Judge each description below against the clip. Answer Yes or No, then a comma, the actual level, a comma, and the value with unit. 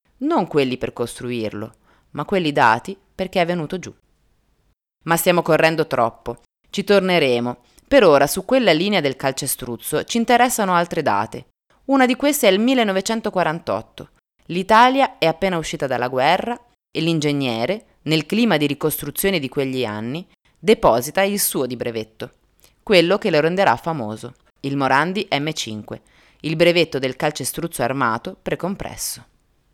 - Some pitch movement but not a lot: No, wide, 6.7 semitones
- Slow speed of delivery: No, average, 135 wpm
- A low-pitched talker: No, medium, 160 Hz